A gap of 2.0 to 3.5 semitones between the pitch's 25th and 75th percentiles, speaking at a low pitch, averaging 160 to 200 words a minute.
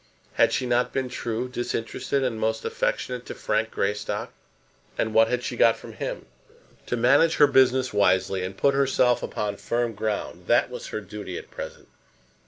Yes: average, 2.9 semitones; low, 120 Hz; average, 175 wpm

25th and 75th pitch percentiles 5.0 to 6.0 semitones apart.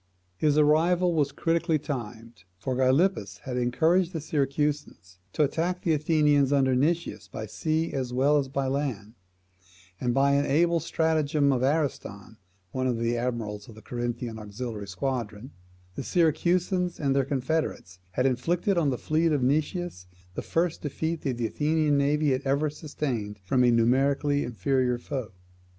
No: average, 4.3 semitones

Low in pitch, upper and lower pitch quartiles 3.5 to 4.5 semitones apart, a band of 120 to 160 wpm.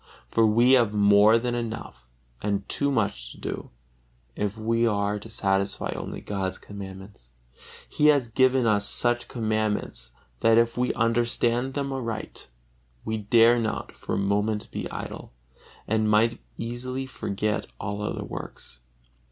No: low, 110 Hz; average, 2.7 semitones; average, 145 wpm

